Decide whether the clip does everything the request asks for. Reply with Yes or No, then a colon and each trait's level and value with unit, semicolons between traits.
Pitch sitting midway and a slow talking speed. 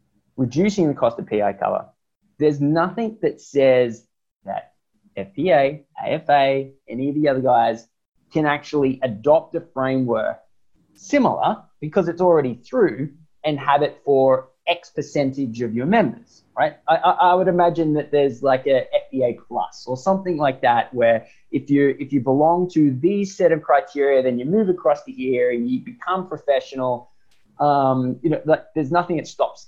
No: medium, 145 Hz; average, 165 wpm